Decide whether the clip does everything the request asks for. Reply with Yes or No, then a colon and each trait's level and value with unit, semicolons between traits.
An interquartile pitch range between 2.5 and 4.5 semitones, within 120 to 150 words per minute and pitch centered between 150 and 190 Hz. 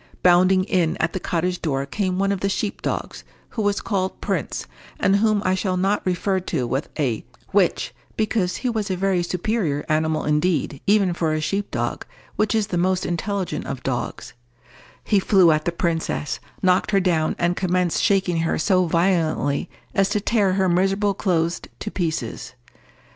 No: average, 3.2 semitones; average, 175 wpm; medium, 185 Hz